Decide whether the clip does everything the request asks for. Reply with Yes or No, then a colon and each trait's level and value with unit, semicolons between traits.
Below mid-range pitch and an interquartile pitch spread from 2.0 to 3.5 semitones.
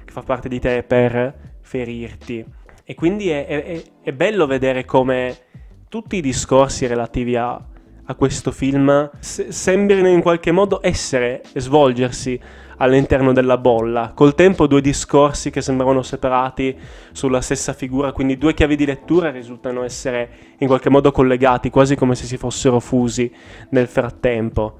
Yes: low, 130 Hz; narrow, 2.4 semitones